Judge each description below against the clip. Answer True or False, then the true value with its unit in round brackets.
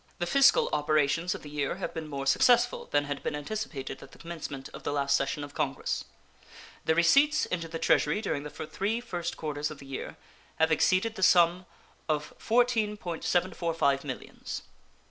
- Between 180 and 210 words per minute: False (170 wpm)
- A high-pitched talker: False (160 Hz)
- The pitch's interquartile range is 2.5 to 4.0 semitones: False (4.4 semitones)